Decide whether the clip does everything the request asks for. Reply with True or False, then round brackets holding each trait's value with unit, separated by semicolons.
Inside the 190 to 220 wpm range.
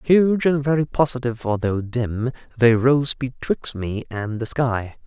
False (155 wpm)